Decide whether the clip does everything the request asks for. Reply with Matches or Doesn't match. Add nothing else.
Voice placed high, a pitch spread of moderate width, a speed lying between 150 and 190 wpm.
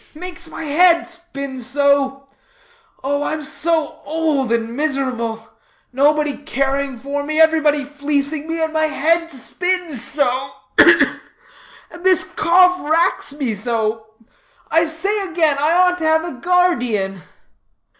Doesn't match